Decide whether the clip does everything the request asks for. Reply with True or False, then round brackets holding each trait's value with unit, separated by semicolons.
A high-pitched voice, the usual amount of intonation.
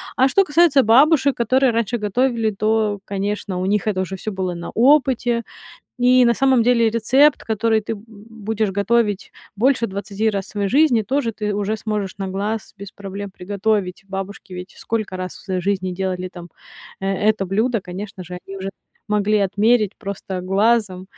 True (210 Hz; 3.2 semitones)